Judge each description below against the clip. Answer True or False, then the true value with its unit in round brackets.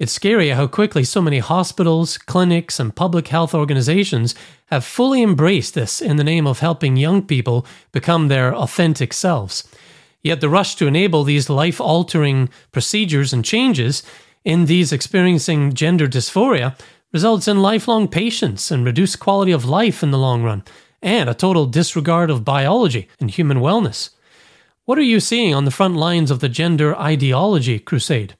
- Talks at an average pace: True (165 wpm)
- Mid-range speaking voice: True (160 Hz)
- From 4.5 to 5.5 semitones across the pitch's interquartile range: True (5.1 semitones)